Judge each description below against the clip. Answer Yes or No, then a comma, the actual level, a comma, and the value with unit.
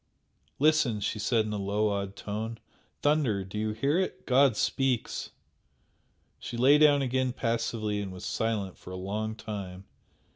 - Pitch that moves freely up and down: No, average, 4.2 semitones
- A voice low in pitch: Yes, low, 110 Hz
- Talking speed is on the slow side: No, average, 155 wpm